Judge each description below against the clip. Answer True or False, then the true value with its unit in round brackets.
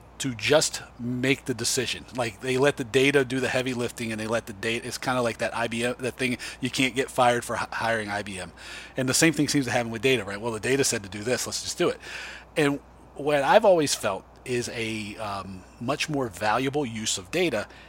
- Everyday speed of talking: False (230 wpm)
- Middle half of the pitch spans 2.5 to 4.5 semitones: True (2.9 semitones)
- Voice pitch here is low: True (120 Hz)